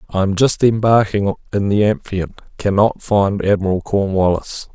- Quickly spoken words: No, average, 140 wpm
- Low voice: Yes, low, 100 Hz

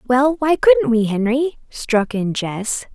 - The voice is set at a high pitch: Yes, high, 245 Hz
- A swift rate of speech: No, average, 165 wpm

